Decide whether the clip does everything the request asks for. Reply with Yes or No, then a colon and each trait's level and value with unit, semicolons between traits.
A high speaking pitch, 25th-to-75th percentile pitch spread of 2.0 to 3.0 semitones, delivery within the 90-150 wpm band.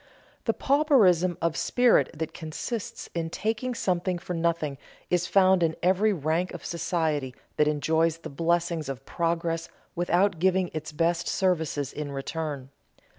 No: medium, 170 Hz; average, 2.7 semitones; average, 140 wpm